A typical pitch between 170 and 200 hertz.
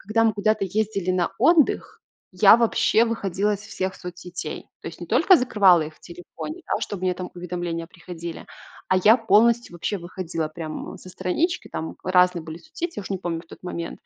Yes: medium, 185 Hz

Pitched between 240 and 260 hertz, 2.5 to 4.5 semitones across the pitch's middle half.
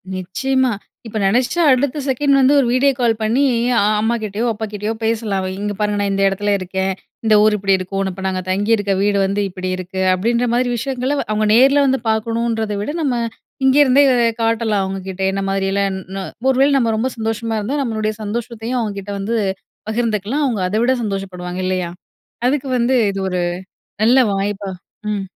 No: high, 215 Hz; average, 3.9 semitones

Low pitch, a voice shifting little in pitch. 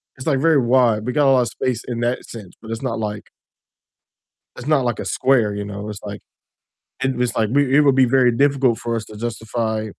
No: low, 120 Hz; average, 3.1 semitones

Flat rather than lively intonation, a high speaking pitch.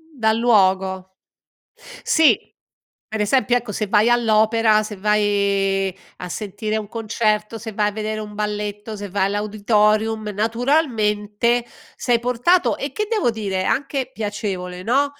Yes: narrow, 2.1 semitones; high, 215 Hz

